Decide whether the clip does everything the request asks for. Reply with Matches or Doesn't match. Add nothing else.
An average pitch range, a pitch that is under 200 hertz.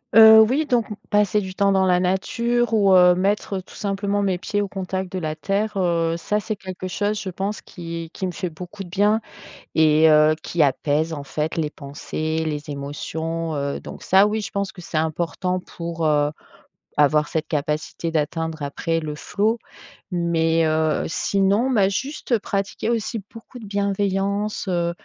Matches